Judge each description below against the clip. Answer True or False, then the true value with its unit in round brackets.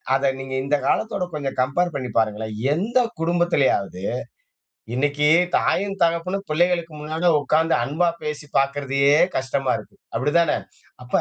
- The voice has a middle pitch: True (150 Hz)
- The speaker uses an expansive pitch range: False (4.2 semitones)